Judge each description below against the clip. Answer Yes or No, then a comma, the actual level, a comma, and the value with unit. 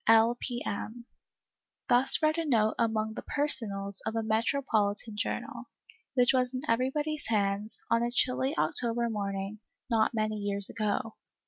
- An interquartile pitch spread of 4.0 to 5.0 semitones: No, average, 3.0 semitones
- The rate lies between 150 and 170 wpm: Yes, average, 160 wpm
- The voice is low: No, high, 225 Hz